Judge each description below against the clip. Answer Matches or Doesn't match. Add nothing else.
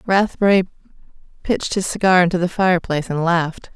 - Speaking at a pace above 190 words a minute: Doesn't match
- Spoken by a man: Doesn't match